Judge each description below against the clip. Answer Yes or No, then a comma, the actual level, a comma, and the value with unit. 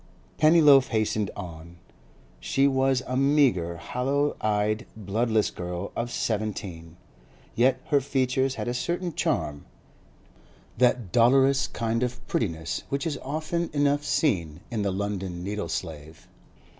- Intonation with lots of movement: Yes, wide, 6.1 semitones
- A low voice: Yes, low, 120 Hz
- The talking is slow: Yes, slow, 120 wpm